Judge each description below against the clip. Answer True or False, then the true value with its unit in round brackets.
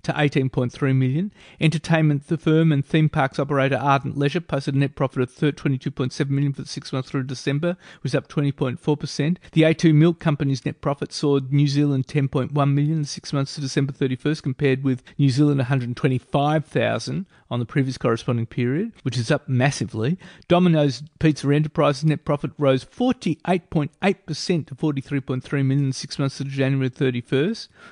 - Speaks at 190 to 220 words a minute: False (170 wpm)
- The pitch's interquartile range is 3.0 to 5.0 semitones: False (2.5 semitones)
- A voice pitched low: False (145 Hz)